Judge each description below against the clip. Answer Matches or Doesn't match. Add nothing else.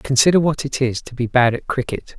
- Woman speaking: Doesn't match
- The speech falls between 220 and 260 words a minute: Matches